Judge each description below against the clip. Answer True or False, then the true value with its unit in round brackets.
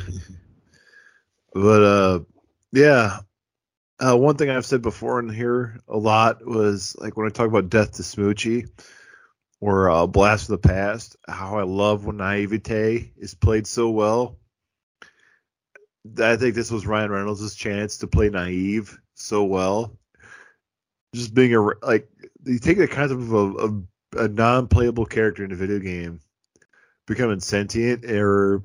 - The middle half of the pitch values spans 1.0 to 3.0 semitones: True (2.6 semitones)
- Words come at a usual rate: True (150 wpm)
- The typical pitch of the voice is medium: False (105 Hz)